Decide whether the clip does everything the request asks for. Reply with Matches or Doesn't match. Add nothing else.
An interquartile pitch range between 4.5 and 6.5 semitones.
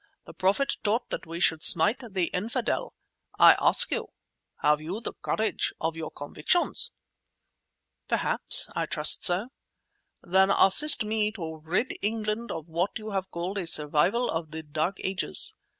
Matches